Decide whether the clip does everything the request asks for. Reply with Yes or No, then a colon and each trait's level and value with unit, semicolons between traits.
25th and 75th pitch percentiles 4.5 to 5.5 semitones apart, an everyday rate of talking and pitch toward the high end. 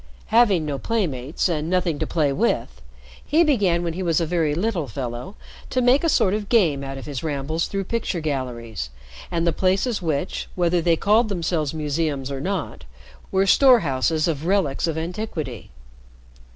No: average, 5.2 semitones; average, 170 wpm; medium, 165 Hz